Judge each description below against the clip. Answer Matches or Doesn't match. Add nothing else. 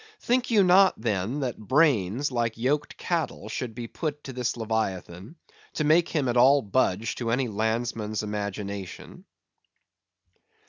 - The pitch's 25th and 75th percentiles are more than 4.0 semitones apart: Matches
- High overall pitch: Doesn't match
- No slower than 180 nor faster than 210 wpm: Doesn't match